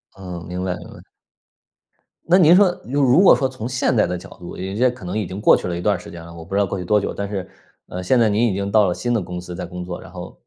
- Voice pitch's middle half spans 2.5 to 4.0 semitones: No, average, 5.3 semitones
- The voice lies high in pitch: No, low, 100 Hz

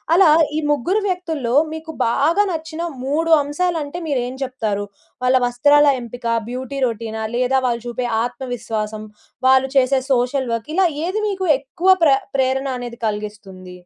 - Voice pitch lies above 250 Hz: Yes, very high, 260 Hz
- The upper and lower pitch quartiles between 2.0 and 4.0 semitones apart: No, average, 4.9 semitones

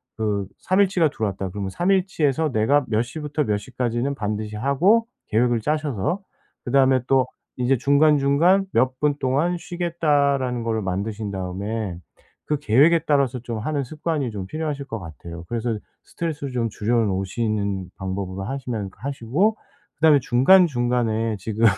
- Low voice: Yes, low, 125 Hz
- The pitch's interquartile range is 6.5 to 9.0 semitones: No, wide, 5.6 semitones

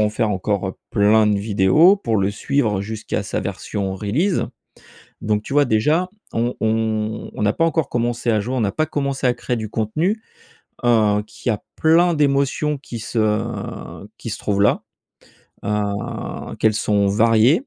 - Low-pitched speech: Yes, low, 110 Hz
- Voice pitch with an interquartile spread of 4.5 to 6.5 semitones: Yes, average, 4.8 semitones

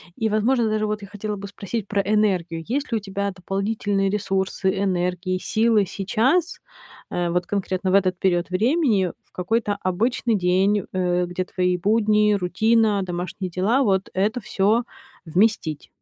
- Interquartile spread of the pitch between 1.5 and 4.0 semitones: Yes, average, 2.8 semitones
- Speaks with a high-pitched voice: Yes, high, 200 Hz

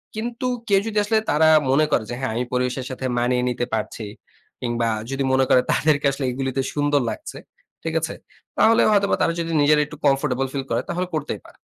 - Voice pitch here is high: No, low, 135 Hz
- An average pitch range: Yes, average, 4.0 semitones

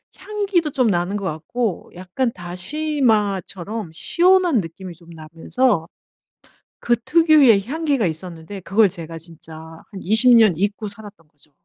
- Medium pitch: No, high, 200 Hz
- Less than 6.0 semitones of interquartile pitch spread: No, wide, 7.1 semitones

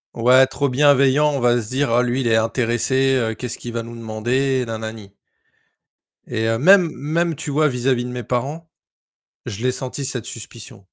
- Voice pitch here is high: No, low, 125 Hz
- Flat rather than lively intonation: No, average, 3.0 semitones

